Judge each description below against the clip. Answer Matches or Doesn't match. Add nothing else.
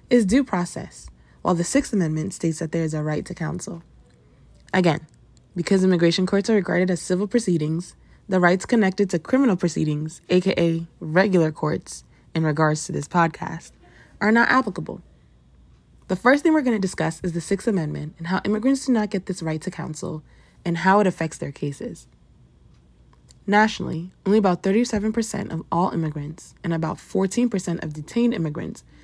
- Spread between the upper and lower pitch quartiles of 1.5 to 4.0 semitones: Matches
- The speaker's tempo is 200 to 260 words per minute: Doesn't match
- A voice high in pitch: Doesn't match